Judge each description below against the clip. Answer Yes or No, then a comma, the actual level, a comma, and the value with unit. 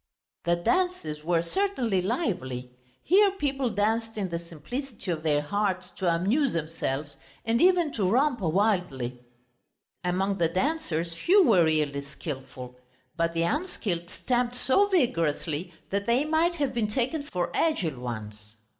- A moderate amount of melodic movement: No, wide, 8.4 semitones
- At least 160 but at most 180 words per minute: No, average, 140 wpm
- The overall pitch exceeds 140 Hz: Yes, high, 190 Hz